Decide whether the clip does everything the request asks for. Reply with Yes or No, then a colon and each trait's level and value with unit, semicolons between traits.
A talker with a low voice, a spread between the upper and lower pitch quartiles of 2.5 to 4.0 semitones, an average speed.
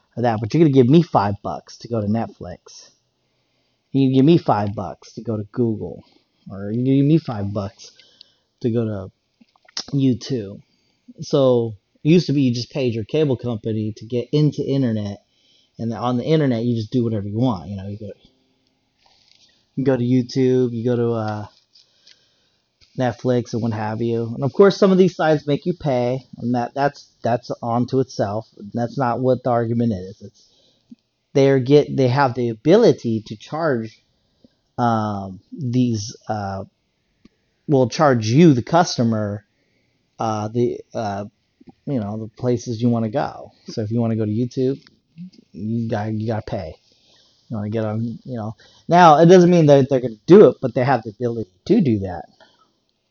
Yes: low, 120 Hz; average, 3.4 semitones; average, 185 wpm